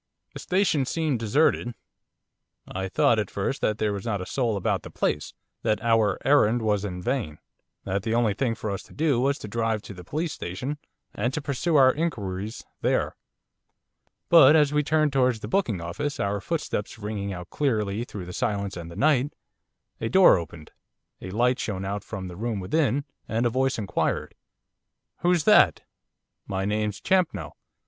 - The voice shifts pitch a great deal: Yes, wide, 5.8 semitones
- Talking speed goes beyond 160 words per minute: Yes, average, 180 wpm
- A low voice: Yes, low, 110 Hz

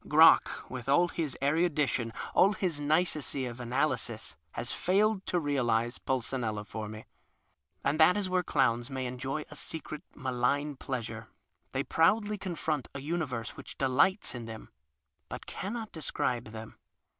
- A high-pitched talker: No, medium, 140 Hz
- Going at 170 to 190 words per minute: No, average, 145 wpm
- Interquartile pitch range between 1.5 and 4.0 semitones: No, average, 5.3 semitones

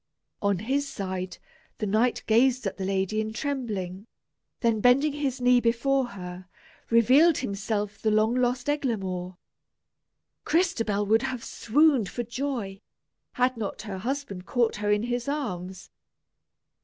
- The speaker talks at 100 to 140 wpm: Yes, slow, 135 wpm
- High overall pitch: Yes, high, 230 Hz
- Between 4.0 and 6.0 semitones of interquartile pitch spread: Yes, average, 4.4 semitones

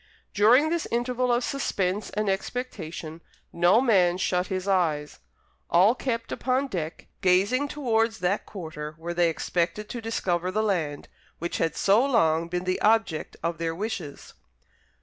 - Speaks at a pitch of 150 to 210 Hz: Yes, high, 190 Hz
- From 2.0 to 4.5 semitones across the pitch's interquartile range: No, average, 5.2 semitones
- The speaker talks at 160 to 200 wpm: No, average, 150 wpm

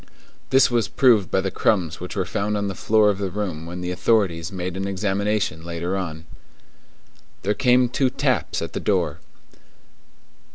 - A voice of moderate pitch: No, low, 100 Hz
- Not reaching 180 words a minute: Yes, average, 170 wpm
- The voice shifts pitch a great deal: No, average, 3.3 semitones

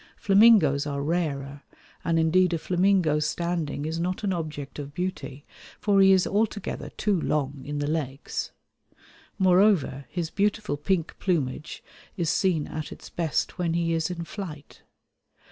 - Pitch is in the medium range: Yes, medium, 165 Hz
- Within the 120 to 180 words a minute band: Yes, average, 145 wpm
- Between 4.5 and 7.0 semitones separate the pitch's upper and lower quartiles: No, average, 4.0 semitones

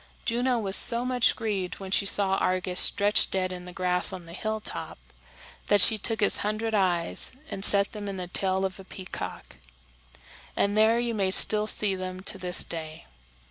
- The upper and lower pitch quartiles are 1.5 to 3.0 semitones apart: Yes, average, 2.7 semitones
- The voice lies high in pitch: Yes, high, 195 Hz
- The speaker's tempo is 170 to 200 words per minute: Yes, average, 185 wpm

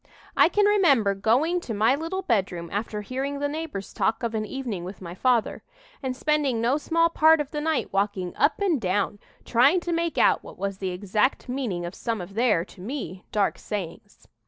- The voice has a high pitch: Yes, high, 235 Hz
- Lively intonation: Yes, wide, 7.0 semitones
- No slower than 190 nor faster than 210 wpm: Yes, average, 200 wpm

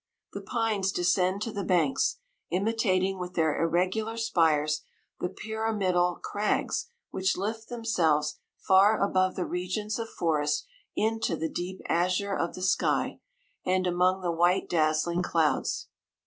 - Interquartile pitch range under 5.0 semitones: Yes, average, 3.3 semitones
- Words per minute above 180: No, slow, 135 wpm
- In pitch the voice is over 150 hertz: Yes, medium, 185 Hz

